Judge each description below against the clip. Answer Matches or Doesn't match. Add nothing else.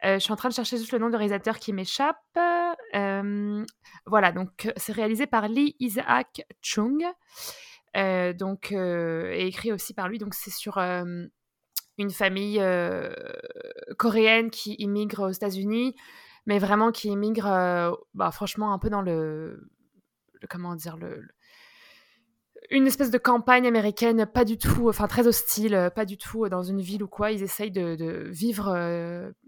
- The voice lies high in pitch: Matches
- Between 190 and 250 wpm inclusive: Doesn't match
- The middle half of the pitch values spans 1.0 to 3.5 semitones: Doesn't match